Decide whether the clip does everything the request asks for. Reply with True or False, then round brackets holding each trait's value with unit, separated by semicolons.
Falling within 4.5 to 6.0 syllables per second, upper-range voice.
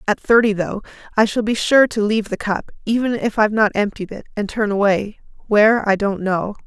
True (5.6 syllables/s; 210 Hz)